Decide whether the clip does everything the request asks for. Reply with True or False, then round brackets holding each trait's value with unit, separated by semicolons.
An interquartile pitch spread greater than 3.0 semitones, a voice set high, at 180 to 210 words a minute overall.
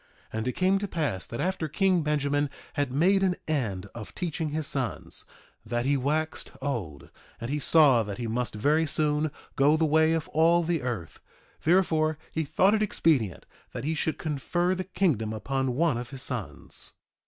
False (4.9 semitones; 150 Hz; 185 wpm)